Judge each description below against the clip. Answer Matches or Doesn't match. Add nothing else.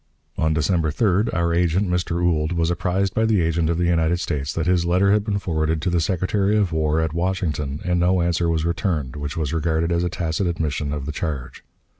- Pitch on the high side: Doesn't match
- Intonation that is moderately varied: Doesn't match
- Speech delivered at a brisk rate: Matches